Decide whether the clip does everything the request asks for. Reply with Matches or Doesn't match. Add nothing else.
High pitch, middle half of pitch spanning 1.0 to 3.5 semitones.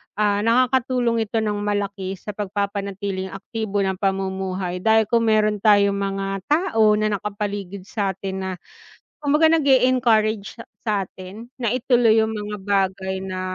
Matches